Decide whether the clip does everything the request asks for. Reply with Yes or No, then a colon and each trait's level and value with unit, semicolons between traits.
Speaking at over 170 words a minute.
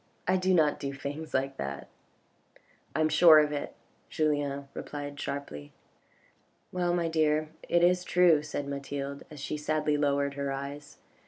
No: average, 160 wpm